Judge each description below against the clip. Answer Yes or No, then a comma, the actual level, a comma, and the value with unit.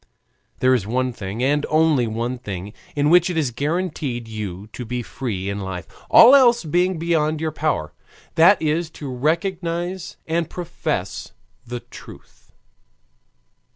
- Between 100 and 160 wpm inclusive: Yes, average, 150 wpm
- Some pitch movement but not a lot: No, wide, 6.1 semitones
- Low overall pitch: No, medium, 145 Hz